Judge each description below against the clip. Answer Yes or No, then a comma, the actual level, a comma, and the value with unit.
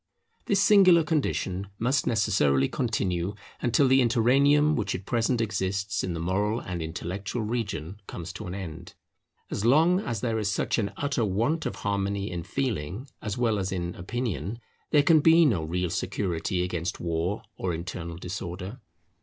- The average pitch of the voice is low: Yes, low, 100 Hz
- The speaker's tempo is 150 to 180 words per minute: Yes, average, 160 wpm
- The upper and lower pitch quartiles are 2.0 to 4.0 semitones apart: No, wide, 5.6 semitones